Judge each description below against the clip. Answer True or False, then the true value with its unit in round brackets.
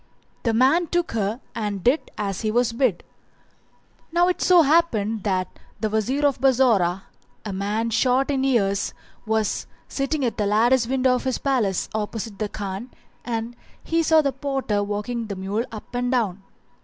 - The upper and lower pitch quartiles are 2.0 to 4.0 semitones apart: False (4.4 semitones)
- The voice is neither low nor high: False (230 Hz)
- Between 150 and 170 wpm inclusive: True (165 wpm)